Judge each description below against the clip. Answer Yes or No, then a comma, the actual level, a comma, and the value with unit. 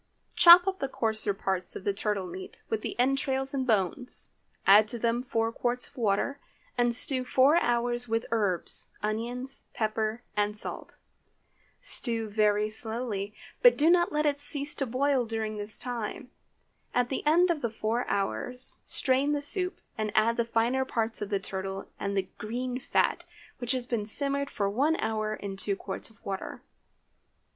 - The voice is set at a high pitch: Yes, high, 230 Hz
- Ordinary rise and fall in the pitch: Yes, average, 3.8 semitones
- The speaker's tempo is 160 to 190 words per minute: Yes, average, 170 wpm